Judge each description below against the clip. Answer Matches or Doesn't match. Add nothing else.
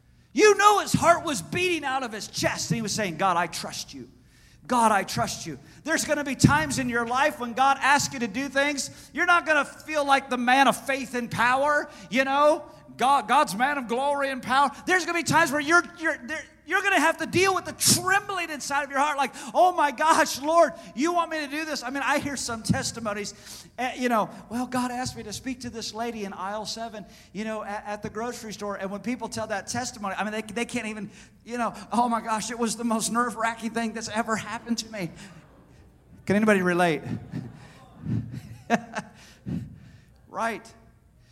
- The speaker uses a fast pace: Matches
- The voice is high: Matches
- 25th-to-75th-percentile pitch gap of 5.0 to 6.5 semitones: Matches